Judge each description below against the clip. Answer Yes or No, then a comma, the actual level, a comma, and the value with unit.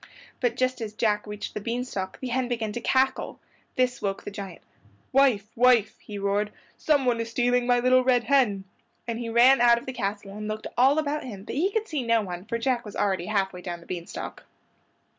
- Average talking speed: No, fast, 220 wpm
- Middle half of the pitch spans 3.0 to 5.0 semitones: Yes, average, 3.7 semitones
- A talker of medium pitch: No, high, 235 Hz